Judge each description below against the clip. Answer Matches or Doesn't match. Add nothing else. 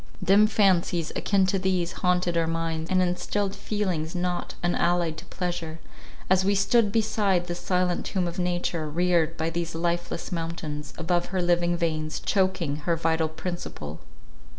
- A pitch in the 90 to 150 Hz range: Doesn't match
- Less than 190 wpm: Matches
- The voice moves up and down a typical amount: Doesn't match